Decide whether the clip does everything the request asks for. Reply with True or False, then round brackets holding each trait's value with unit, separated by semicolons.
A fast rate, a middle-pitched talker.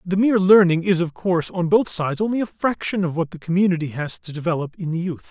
True (250 wpm; 175 Hz)